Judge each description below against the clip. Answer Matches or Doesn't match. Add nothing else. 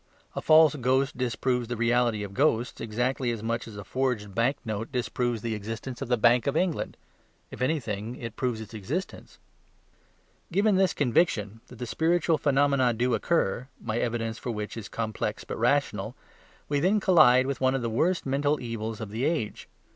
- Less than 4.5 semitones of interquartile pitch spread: Matches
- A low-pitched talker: Matches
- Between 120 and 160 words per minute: Doesn't match